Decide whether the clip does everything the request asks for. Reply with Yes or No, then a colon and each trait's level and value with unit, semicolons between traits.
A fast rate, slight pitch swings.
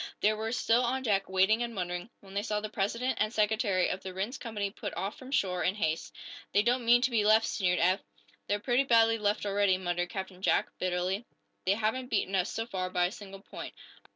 No: fast, 220 wpm; average, 3.2 semitones